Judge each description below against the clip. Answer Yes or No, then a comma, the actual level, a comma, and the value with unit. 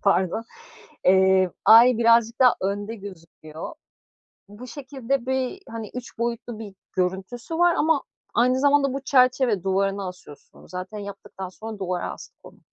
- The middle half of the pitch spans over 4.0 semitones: Yes, average, 4.9 semitones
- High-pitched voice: Yes, high, 220 Hz